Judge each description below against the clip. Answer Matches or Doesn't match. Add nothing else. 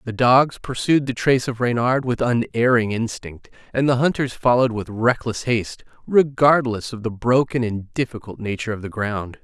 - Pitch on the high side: Doesn't match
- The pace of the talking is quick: Doesn't match